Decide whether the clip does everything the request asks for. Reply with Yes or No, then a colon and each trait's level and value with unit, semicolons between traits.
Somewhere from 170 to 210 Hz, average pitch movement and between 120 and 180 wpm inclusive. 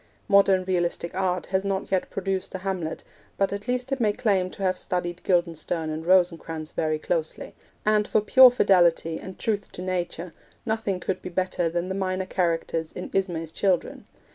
No: medium, 185 Hz; narrow, 2.3 semitones; average, 175 wpm